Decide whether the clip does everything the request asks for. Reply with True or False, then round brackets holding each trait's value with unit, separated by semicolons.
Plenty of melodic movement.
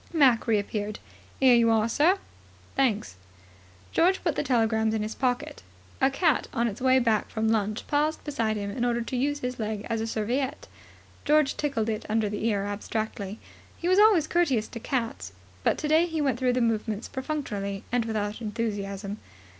False (4.1 semitones)